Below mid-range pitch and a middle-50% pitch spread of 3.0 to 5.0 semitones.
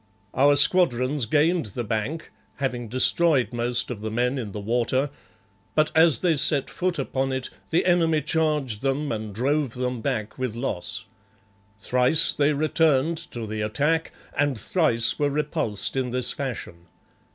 Yes: low, 130 Hz; average, 4.4 semitones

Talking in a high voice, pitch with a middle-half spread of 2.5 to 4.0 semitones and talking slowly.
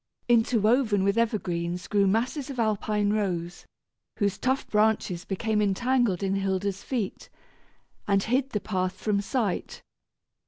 Yes: high, 210 Hz; average, 3.1 semitones; slow, 125 wpm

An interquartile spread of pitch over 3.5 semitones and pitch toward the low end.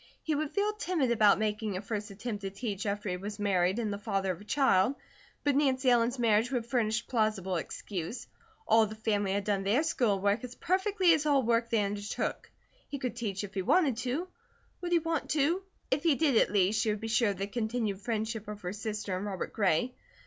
No: average, 4.2 semitones; high, 220 Hz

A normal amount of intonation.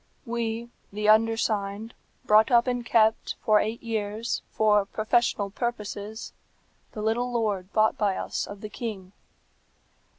No: narrow, 1.9 semitones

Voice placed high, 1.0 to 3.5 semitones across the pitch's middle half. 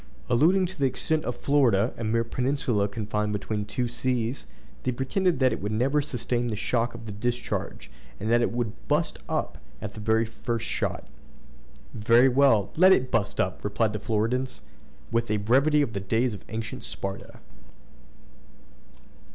No: low, 115 Hz; average, 3.2 semitones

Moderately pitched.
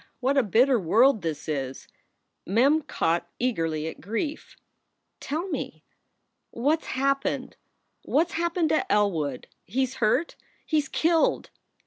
No: very high, 255 Hz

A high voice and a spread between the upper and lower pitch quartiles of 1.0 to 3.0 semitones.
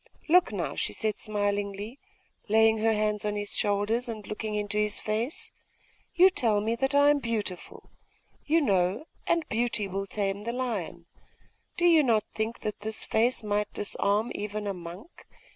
Yes: high, 215 Hz; narrow, 2.5 semitones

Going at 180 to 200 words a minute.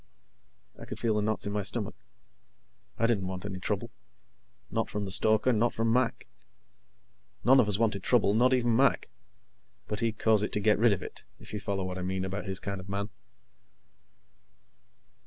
Yes: average, 190 wpm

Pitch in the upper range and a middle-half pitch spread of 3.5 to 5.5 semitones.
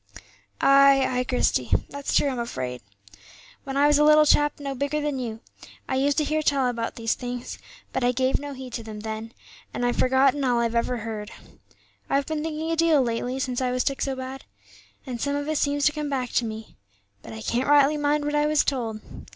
No: very high, 265 Hz; average, 3.0 semitones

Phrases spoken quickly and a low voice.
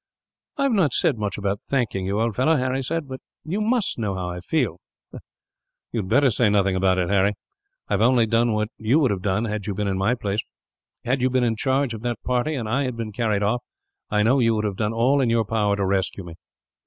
Yes: fast, 245 wpm; low, 115 Hz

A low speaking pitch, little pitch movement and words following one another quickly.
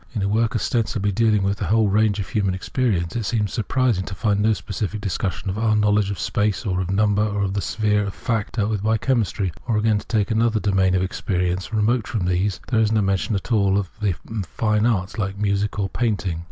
Yes: low, 105 Hz; narrow, 2.2 semitones; fast, 230 wpm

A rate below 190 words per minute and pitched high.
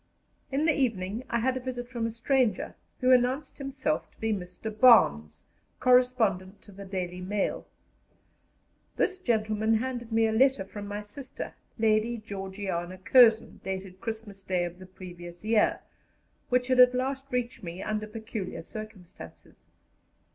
Yes: average, 145 wpm; high, 220 Hz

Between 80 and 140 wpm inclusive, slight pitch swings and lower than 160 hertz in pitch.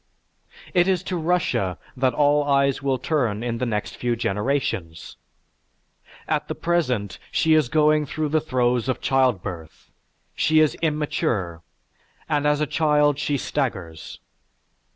No: slow, 135 wpm; average, 4.7 semitones; medium, 140 Hz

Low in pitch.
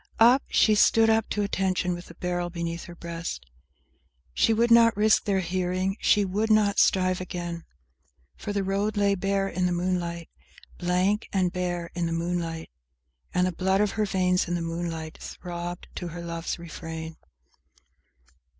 No: medium, 180 Hz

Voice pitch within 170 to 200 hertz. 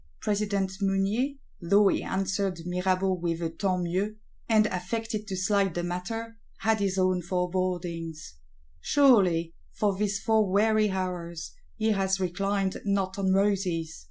Yes: high, 190 Hz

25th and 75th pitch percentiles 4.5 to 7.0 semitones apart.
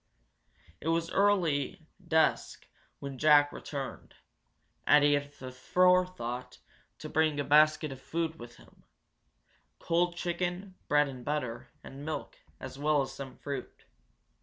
No: average, 3.4 semitones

